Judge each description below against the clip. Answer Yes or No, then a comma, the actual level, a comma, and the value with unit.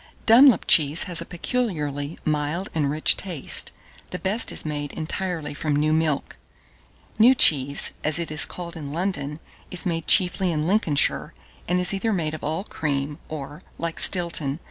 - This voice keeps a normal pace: Yes, average, 165 wpm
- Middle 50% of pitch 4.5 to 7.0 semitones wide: No, average, 3.5 semitones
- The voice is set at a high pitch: No, medium, 160 Hz